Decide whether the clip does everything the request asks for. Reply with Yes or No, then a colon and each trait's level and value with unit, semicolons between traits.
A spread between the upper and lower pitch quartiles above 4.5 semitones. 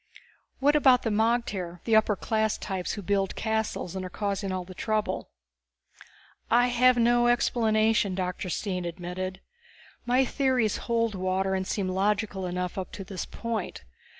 No: average, 3.7 semitones